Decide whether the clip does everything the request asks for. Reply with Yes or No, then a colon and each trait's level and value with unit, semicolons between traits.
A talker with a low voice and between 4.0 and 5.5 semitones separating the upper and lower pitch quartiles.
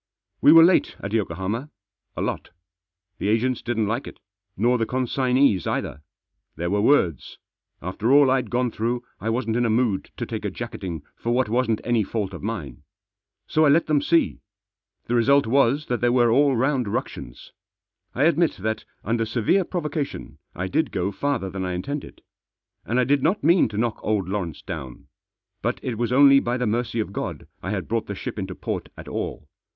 Yes: low, 120 Hz; average, 4.9 semitones